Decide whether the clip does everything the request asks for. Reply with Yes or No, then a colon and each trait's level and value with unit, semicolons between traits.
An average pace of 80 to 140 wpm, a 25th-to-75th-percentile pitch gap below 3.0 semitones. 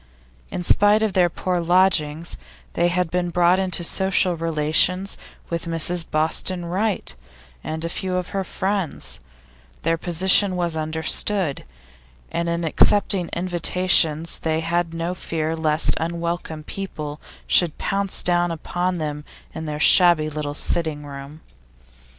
Yes: slow, 135 wpm; narrow, 2.4 semitones